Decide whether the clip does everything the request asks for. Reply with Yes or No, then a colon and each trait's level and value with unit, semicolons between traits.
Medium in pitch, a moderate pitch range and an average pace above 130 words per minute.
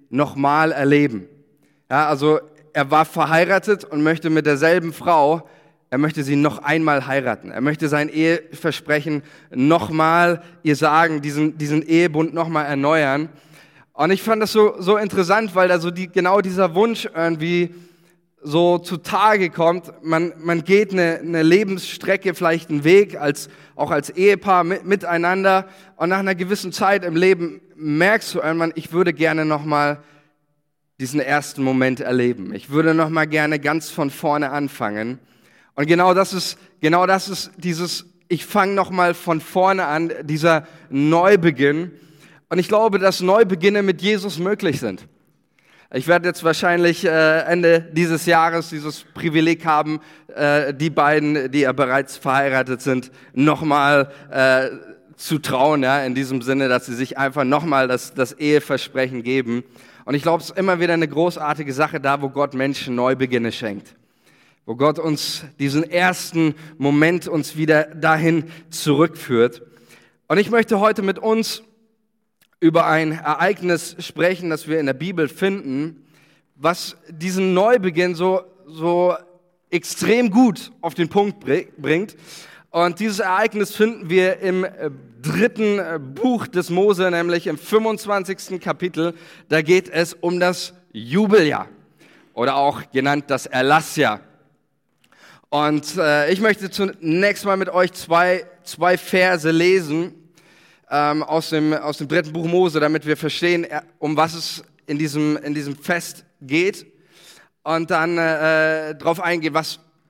Yes: medium, 165 Hz; average, 3.4 semitones; average, 145 wpm